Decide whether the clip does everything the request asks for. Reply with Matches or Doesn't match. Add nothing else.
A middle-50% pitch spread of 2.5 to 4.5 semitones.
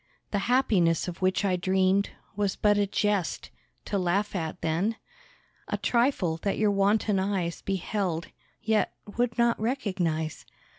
Matches